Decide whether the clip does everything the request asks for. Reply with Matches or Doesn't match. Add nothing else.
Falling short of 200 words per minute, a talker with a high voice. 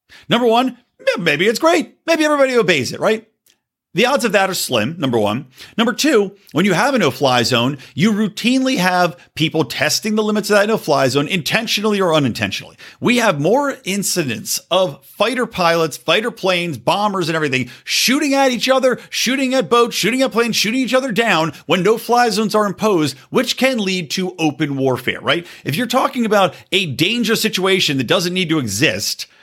Matches